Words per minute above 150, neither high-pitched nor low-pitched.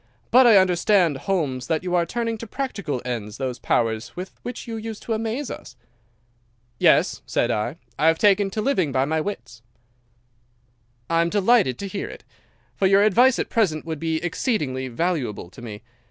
Yes: average, 180 wpm; medium, 175 Hz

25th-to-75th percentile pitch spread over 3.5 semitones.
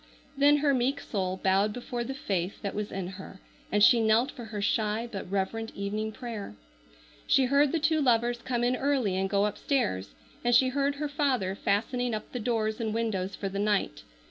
Yes: average, 4.2 semitones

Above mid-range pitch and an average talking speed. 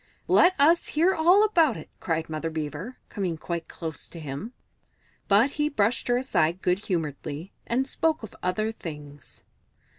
Yes: high, 200 Hz; average, 155 wpm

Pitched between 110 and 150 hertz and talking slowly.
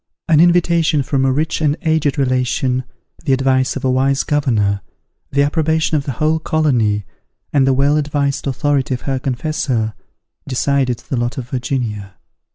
No: low, 135 Hz; average, 160 wpm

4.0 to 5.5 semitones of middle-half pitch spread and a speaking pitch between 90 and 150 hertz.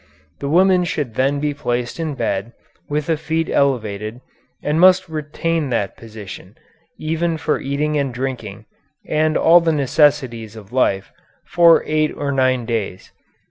Yes: average, 5.1 semitones; medium, 140 Hz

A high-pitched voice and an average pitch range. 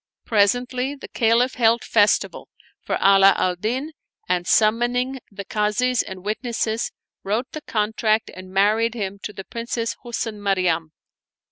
Yes: high, 220 Hz; average, 3.3 semitones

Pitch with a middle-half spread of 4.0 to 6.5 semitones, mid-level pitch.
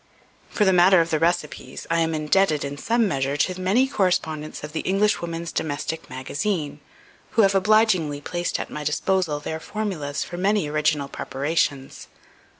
Yes: average, 4.4 semitones; medium, 165 Hz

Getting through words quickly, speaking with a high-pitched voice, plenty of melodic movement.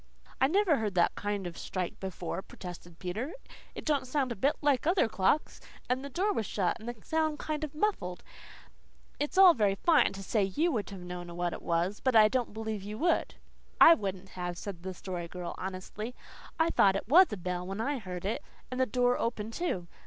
Yes: fast, 215 wpm; high, 215 Hz; wide, 7.2 semitones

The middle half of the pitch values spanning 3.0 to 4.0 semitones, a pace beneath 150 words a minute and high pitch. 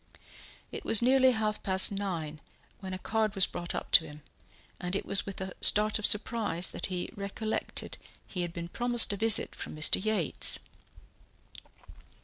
No: average, 3.5 semitones; average, 165 wpm; high, 200 Hz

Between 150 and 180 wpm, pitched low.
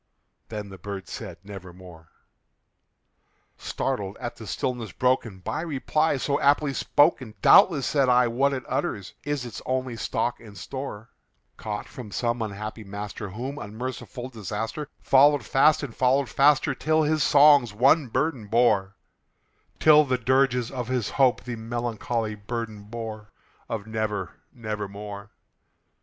No: slow, 135 wpm; low, 120 Hz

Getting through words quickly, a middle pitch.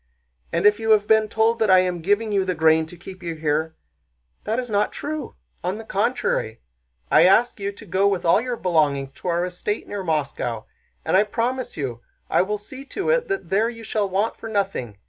No: fast, 210 wpm; high, 195 Hz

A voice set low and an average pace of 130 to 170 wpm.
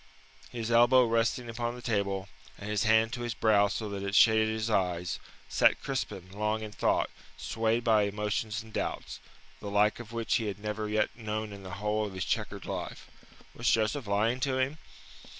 No: low, 110 Hz; average, 190 wpm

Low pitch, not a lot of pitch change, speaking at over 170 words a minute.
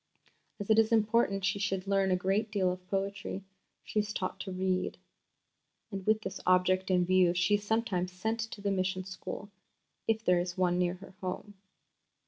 No: high, 190 Hz; narrow, 2.1 semitones; average, 185 wpm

